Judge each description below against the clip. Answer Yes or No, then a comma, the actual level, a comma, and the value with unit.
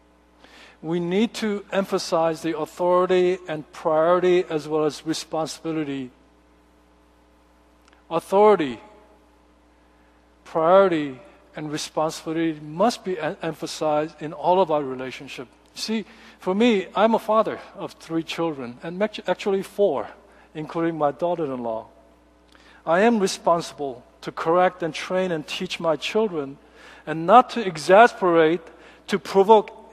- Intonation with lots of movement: No, average, 4.8 semitones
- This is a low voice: No, medium, 165 Hz